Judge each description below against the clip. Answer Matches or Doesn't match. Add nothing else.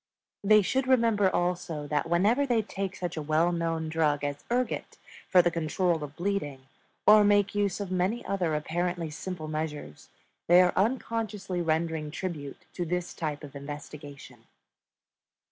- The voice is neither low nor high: Matches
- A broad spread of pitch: Doesn't match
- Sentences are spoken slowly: Doesn't match